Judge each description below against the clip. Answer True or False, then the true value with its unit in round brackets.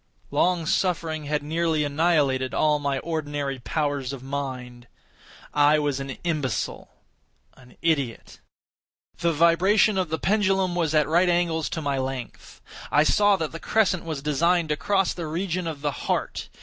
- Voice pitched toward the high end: False (155 Hz)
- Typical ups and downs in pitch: True (3.4 semitones)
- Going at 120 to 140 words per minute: False (150 wpm)